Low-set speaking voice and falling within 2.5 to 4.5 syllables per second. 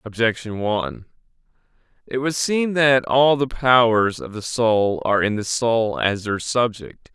Yes: low, 120 Hz; 4.1 syllables/s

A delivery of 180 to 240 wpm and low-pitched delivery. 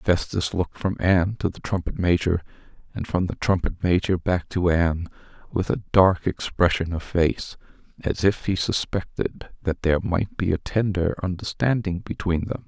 No: average, 165 wpm; very low, 90 Hz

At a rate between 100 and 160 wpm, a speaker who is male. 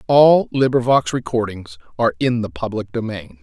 Yes: average, 140 wpm; male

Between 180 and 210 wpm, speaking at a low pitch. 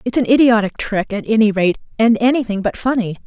No: average, 200 wpm; high, 225 Hz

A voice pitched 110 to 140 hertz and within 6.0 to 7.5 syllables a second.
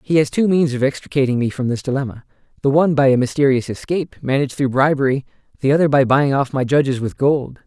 Yes: low, 135 Hz; 6.5 syllables/s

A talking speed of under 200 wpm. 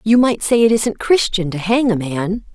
No: fast, 235 wpm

